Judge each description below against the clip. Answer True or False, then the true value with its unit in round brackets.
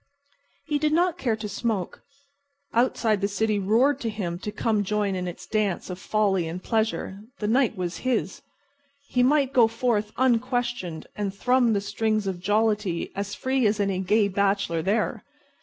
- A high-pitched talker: True (210 Hz)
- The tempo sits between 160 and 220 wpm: True (170 wpm)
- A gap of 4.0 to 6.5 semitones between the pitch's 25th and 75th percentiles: False (3.4 semitones)